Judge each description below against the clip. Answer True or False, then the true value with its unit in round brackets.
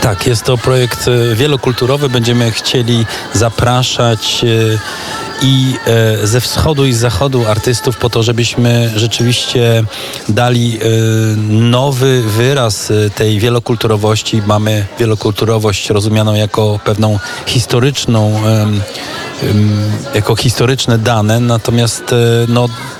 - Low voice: True (115 Hz)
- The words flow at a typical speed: False (90 wpm)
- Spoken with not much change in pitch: True (2.2 semitones)